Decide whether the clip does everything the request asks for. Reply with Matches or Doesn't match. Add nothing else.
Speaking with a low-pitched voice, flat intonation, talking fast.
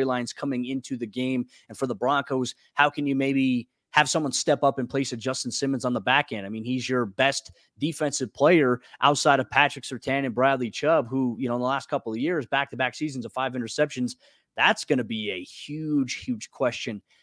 Matches